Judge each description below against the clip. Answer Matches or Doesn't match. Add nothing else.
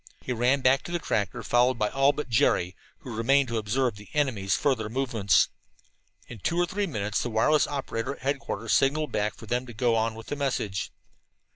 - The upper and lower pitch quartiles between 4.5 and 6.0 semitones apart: Doesn't match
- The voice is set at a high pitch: Doesn't match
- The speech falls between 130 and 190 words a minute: Doesn't match